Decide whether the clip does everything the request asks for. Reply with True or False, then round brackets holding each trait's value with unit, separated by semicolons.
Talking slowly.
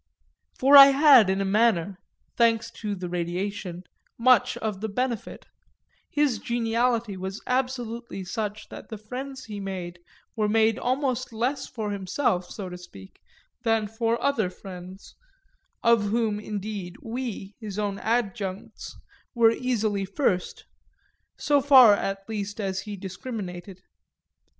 True (130 wpm)